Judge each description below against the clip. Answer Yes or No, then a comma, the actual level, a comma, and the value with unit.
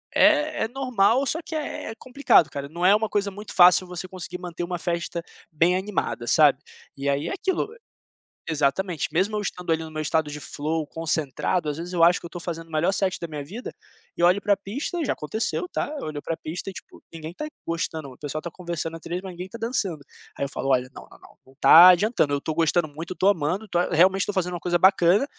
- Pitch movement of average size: Yes, average, 3.8 semitones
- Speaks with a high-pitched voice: No, medium, 175 Hz